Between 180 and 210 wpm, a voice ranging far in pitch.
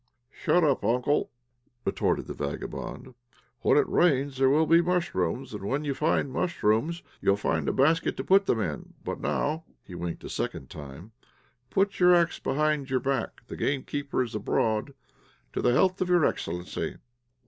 No: average, 170 wpm; wide, 7.4 semitones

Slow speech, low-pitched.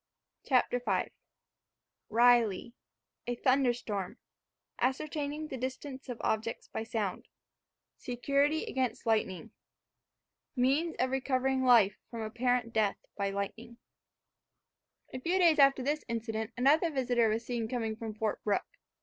No: slow, 120 wpm; high, 245 Hz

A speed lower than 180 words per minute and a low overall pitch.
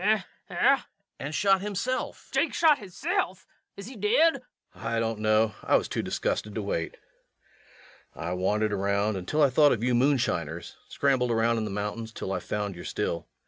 No: average, 185 wpm; low, 115 Hz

